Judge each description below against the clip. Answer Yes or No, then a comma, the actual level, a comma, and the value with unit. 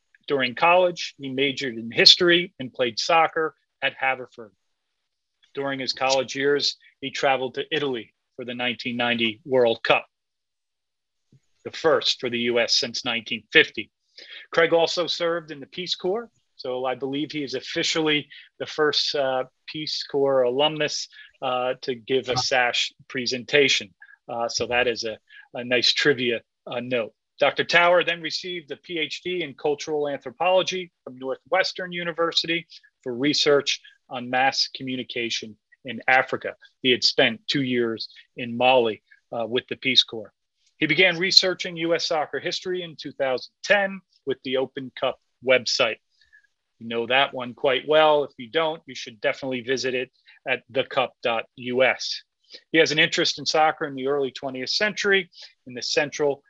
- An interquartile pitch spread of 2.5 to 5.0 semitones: Yes, average, 4.7 semitones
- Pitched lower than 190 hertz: Yes, medium, 140 Hz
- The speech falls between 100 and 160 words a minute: Yes, average, 150 wpm